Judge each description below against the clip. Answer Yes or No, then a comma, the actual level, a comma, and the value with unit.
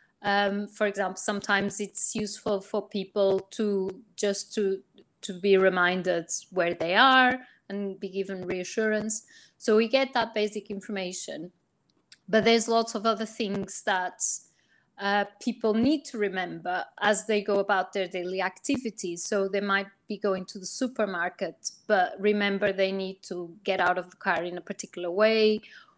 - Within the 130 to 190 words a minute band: Yes, average, 155 wpm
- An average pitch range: No, narrow, 2.2 semitones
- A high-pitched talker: Yes, high, 200 Hz